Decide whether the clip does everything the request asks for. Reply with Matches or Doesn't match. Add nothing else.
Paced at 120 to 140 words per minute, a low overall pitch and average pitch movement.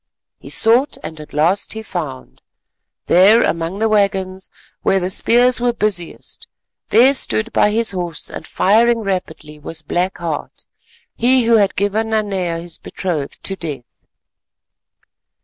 Doesn't match